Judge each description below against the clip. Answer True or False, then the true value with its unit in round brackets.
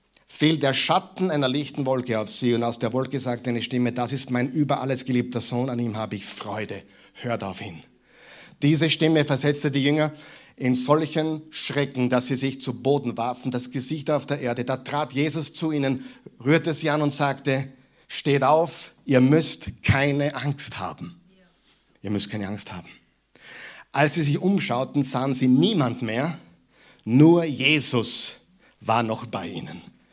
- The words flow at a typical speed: True (170 wpm)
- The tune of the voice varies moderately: True (3.8 semitones)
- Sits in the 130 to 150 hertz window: True (135 Hz)